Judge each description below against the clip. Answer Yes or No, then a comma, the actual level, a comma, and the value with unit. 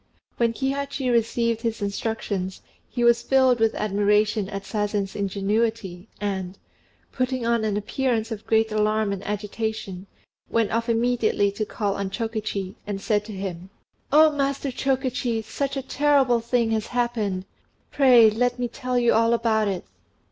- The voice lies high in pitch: Yes, high, 225 Hz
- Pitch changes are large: No, average, 2.9 semitones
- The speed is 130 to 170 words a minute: Yes, average, 150 wpm